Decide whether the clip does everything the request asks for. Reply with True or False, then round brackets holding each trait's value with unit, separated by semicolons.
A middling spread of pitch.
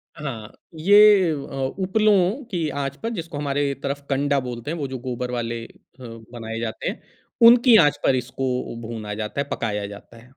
False (6.1 semitones)